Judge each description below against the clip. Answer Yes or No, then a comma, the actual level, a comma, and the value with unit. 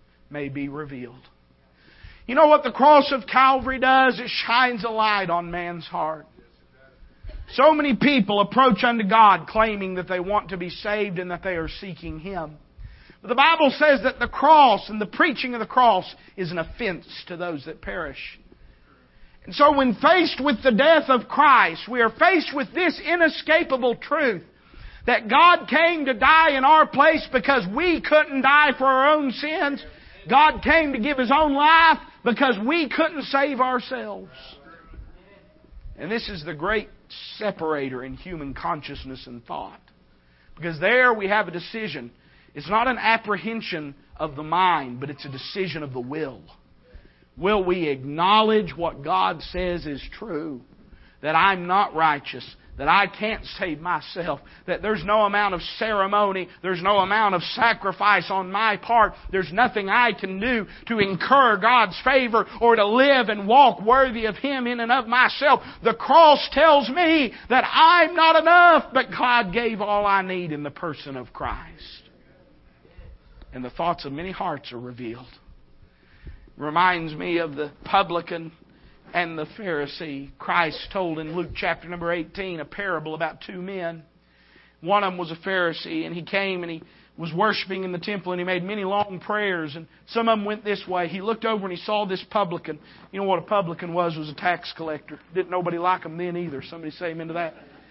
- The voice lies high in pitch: Yes, high, 195 Hz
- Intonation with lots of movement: Yes, wide, 7.0 semitones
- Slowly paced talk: No, average, 180 wpm